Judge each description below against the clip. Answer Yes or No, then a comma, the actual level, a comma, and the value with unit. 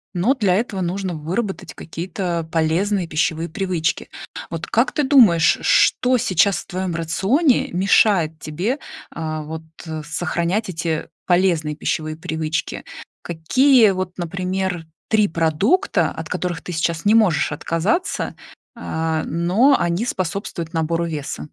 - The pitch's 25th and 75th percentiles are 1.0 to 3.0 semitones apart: No, average, 3.7 semitones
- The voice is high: No, medium, 175 Hz